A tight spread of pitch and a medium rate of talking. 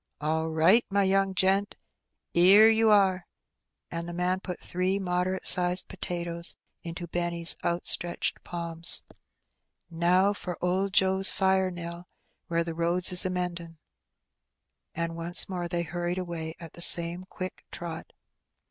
Yes: narrow, 1.8 semitones; average, 150 wpm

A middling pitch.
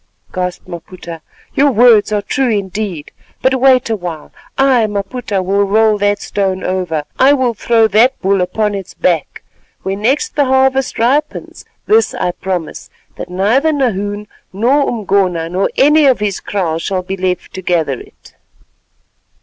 No: high, 205 Hz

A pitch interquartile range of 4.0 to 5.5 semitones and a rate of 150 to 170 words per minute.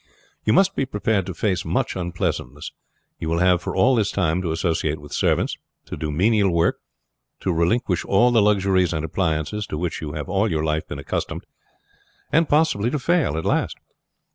No: average, 5.1 semitones; average, 190 wpm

